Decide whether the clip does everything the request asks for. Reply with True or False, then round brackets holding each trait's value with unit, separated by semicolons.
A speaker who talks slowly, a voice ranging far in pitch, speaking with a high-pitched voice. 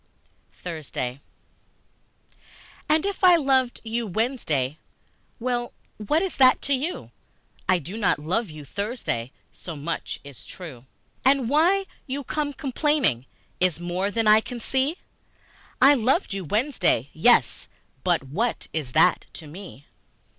True (130 wpm; 8.6 semitones; 220 Hz)